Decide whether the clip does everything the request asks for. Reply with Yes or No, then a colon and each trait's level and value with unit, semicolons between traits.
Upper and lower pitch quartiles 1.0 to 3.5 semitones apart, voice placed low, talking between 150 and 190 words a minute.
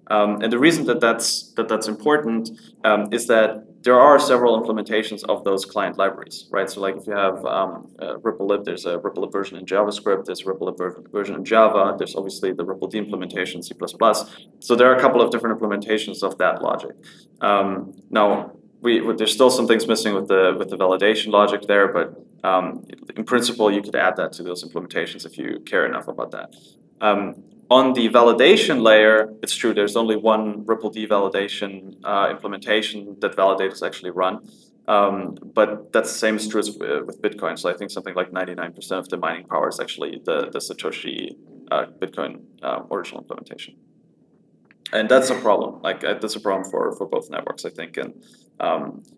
No: average, 2.7 semitones; low, 110 Hz; average, 200 wpm